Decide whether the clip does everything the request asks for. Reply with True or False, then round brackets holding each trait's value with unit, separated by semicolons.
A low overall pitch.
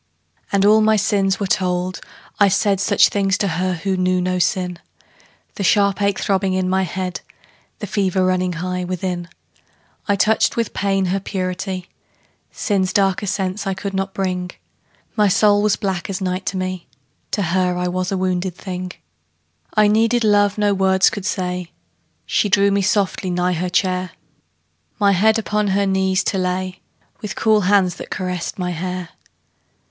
False (190 Hz)